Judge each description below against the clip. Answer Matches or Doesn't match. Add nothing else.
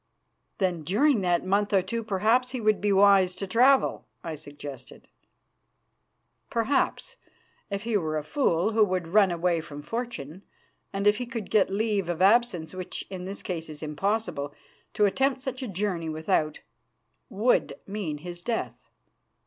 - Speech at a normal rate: Matches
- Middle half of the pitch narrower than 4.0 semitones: Doesn't match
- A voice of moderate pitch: Doesn't match